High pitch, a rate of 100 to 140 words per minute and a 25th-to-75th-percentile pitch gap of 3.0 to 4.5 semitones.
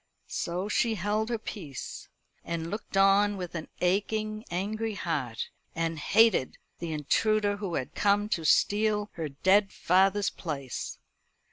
Yes: high, 195 Hz; slow, 135 wpm; average, 4.0 semitones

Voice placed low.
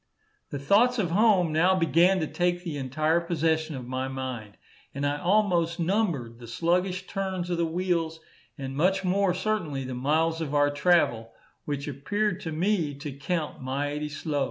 No: medium, 165 Hz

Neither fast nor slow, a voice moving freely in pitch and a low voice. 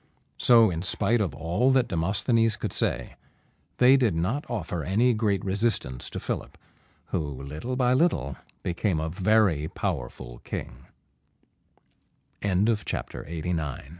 No: slow, 110 wpm; wide, 6.5 semitones; low, 100 Hz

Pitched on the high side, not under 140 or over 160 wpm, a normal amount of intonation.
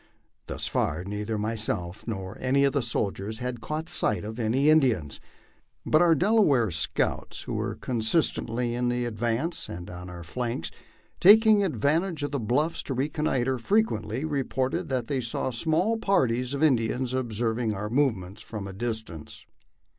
No: low, 120 Hz; average, 155 wpm; average, 4.9 semitones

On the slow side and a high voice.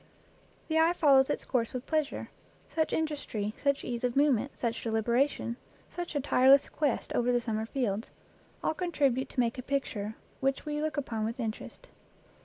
No: average, 175 wpm; very high, 265 Hz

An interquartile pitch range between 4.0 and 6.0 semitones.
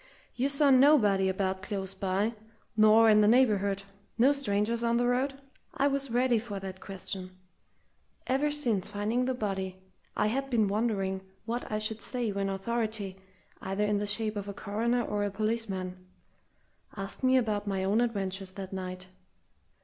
No: average, 3.6 semitones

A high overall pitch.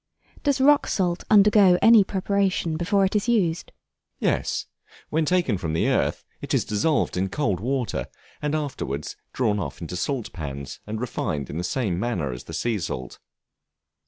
No: low, 135 Hz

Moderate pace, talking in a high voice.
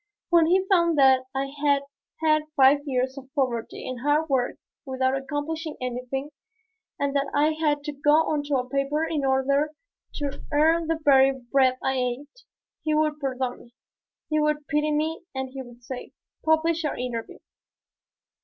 Yes: average, 165 wpm; very high, 285 Hz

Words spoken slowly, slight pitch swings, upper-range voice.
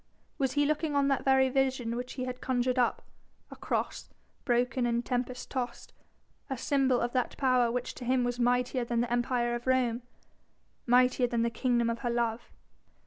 No: average, 185 wpm; narrow, 1.5 semitones; very high, 250 Hz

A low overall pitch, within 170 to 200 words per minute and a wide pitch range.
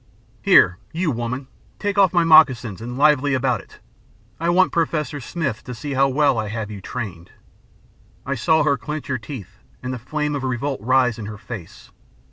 No: low, 130 Hz; average, 185 wpm; average, 4.5 semitones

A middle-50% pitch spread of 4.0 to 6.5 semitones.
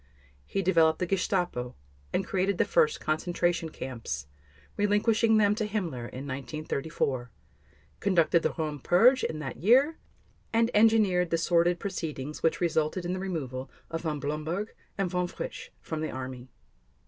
Yes: average, 4.7 semitones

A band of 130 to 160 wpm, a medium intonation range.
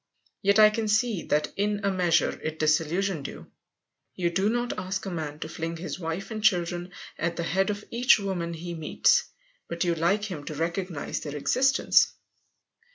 No: average, 180 wpm; average, 3.8 semitones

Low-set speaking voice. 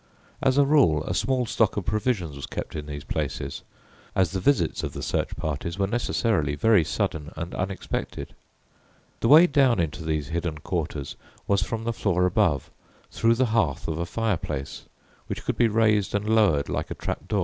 Yes: very low, 95 Hz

